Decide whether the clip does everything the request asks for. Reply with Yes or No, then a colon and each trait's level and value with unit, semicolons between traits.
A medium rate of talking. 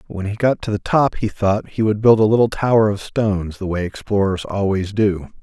No: fast, 230 wpm